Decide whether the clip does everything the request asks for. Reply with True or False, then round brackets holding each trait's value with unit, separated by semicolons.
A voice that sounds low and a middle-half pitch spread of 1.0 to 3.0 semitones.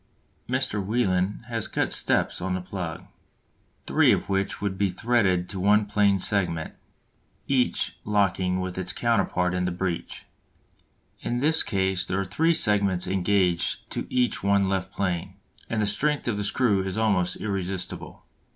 True (100 Hz; 2.6 semitones)